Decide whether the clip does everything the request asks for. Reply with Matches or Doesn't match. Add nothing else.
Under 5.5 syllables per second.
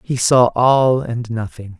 Matches